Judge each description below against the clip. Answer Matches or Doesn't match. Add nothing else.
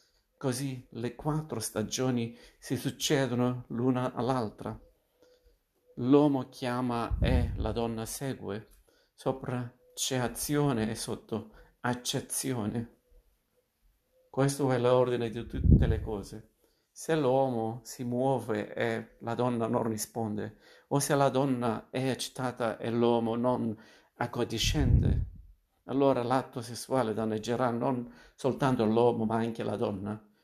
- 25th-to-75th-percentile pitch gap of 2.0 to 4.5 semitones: Matches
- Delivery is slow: Matches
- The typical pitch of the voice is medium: Doesn't match